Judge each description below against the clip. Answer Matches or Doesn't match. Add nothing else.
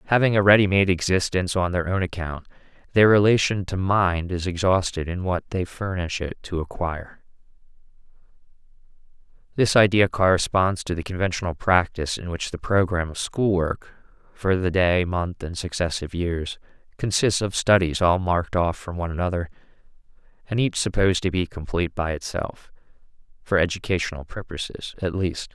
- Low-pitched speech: Matches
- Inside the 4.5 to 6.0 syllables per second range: Matches